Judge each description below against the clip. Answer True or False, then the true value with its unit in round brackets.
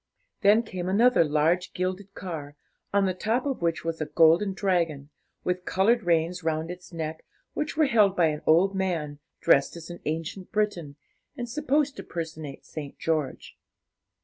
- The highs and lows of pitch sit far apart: False (4.0 semitones)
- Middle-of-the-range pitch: True (175 Hz)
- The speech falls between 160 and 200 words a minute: True (165 wpm)